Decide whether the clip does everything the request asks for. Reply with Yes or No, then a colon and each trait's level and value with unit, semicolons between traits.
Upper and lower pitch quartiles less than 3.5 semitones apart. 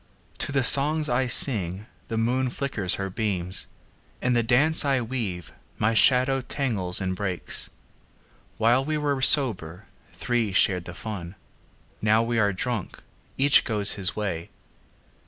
No: wide, 5.4 semitones